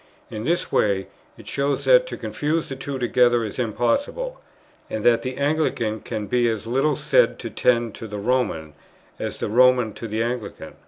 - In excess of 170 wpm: Yes, average, 180 wpm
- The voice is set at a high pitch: No, low, 120 Hz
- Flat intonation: No, average, 4.1 semitones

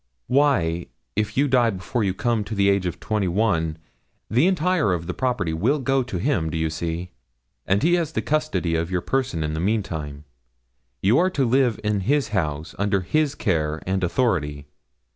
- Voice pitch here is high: No, low, 100 Hz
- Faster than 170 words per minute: Yes, average, 190 wpm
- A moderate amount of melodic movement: No, wide, 7.7 semitones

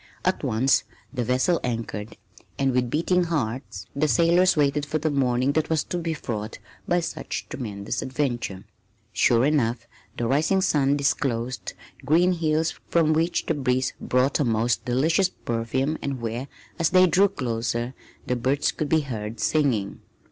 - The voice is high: No, low, 135 Hz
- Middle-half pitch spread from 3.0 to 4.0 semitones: No, average, 4.9 semitones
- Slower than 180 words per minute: Yes, average, 155 wpm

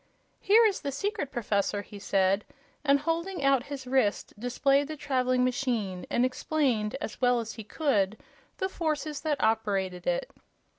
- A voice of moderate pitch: No, very high, 255 Hz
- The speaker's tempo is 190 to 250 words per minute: No, average, 155 wpm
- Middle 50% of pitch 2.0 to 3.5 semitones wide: No, wide, 5.6 semitones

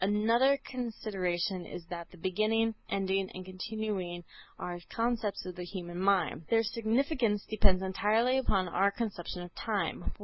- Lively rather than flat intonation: No, average, 3.7 semitones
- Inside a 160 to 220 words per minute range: No, average, 140 wpm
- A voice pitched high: Yes, high, 200 Hz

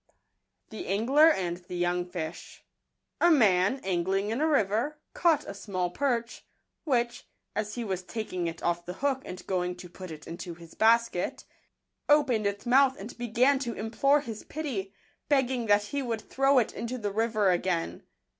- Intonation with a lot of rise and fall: Yes, wide, 5.9 semitones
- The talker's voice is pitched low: No, high, 215 Hz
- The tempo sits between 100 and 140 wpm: No, average, 165 wpm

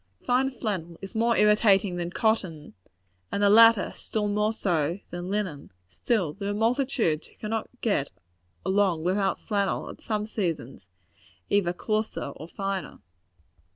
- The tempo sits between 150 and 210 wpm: No, slow, 135 wpm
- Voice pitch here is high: Yes, high, 200 Hz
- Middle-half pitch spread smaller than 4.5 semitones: Yes, average, 3.7 semitones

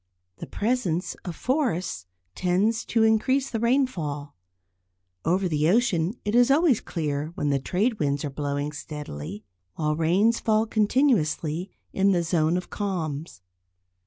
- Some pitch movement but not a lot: No, wide, 6.7 semitones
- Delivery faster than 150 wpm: No, slow, 135 wpm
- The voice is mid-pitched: Yes, medium, 180 Hz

